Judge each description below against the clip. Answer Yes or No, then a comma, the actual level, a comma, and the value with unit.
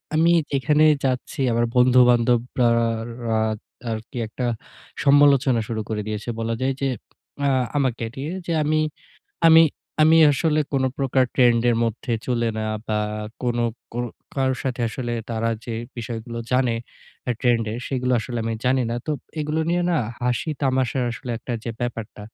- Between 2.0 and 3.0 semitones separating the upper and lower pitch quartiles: Yes, narrow, 2.6 semitones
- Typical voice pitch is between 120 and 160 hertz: Yes, low, 125 Hz